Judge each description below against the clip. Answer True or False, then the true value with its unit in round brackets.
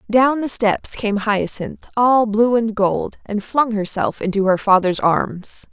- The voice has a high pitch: True (215 Hz)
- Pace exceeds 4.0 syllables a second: False (3.7 syllables/s)